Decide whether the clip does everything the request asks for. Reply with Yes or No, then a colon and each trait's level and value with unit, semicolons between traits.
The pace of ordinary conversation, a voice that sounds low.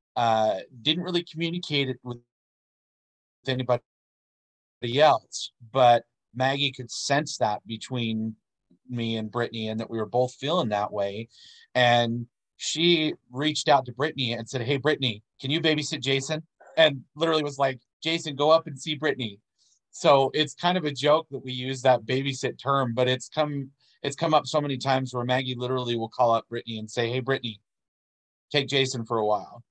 Yes: average, 175 wpm; low, 130 Hz